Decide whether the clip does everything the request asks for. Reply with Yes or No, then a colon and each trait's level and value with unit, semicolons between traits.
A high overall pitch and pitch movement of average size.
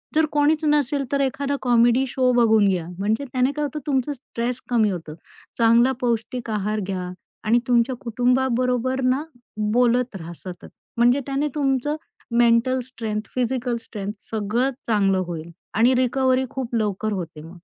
Yes: high, 240 Hz; average, 3.4 semitones